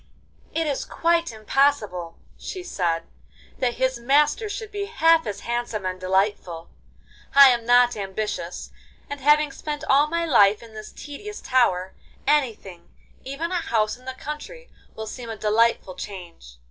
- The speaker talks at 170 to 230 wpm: No, average, 145 wpm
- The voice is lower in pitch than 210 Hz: No, high, 245 Hz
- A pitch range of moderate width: No, wide, 6.4 semitones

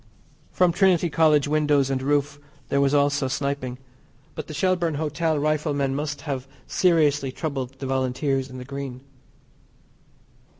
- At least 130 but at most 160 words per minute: Yes, slow, 135 wpm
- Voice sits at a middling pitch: Yes, medium, 145 Hz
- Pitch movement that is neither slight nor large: No, narrow, 2.3 semitones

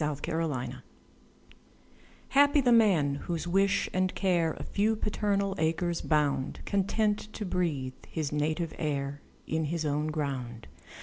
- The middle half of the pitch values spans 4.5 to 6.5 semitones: Yes, average, 5.1 semitones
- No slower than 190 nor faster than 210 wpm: No, slow, 135 wpm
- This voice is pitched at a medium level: Yes, medium, 165 Hz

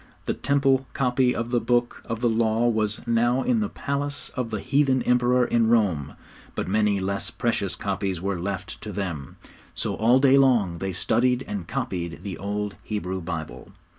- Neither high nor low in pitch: No, low, 115 Hz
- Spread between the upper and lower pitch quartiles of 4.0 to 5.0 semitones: Yes, average, 4.3 semitones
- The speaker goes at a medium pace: Yes, average, 175 wpm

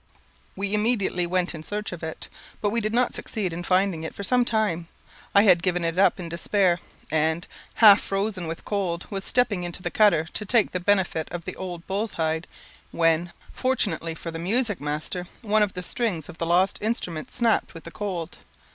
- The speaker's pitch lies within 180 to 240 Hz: Yes, medium, 185 Hz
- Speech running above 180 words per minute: Yes, average, 200 wpm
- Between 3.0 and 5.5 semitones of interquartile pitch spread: Yes, average, 3.7 semitones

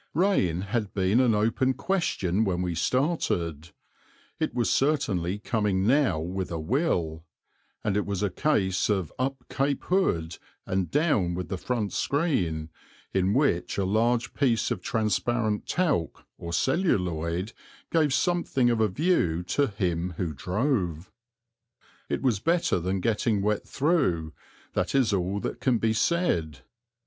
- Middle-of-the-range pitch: No, low, 105 Hz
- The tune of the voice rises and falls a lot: Yes, wide, 7.0 semitones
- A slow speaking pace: No, average, 145 wpm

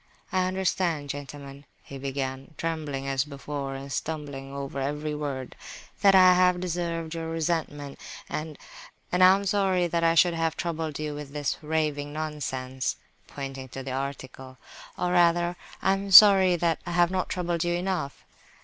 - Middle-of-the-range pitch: Yes, medium, 155 Hz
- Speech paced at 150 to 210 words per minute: Yes, average, 155 wpm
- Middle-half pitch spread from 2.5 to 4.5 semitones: Yes, average, 4.0 semitones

